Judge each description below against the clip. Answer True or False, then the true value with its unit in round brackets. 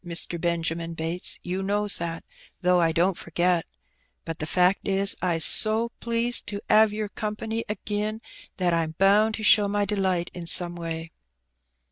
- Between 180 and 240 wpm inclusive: False (160 wpm)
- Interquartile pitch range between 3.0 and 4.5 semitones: True (3.7 semitones)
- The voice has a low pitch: False (185 Hz)